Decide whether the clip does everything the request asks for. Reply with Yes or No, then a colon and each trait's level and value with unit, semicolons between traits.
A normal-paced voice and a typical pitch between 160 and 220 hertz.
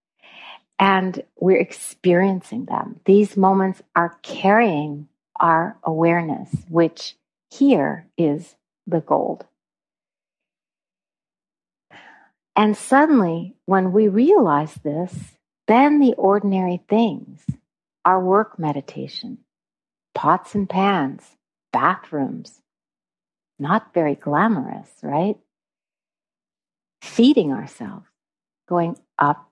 No: slow, 80 wpm; high, 190 Hz